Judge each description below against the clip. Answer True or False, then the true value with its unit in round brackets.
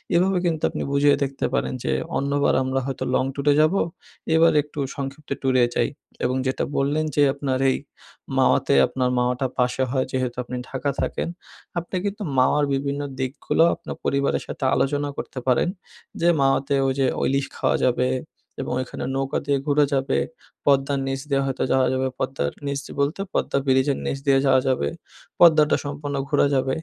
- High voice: False (135 Hz)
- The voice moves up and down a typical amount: False (1.6 semitones)